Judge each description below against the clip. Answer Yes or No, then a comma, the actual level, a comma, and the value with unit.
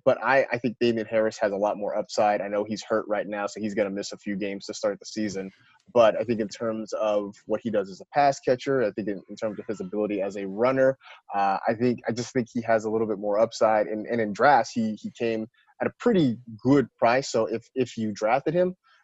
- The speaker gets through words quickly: Yes, fast, 265 wpm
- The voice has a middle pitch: No, low, 110 Hz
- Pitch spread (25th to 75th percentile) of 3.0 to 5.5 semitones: No, narrow, 2.6 semitones